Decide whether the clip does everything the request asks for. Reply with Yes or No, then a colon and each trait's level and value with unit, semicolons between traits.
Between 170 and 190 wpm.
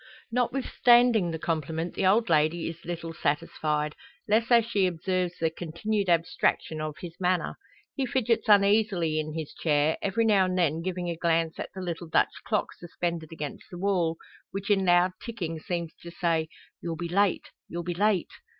Yes: average, 175 wpm